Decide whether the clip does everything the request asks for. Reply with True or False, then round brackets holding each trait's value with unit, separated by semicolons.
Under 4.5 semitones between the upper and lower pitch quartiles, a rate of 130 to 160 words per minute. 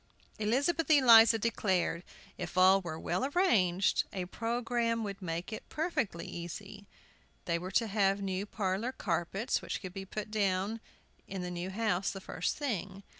True (3.7 semitones; 155 wpm)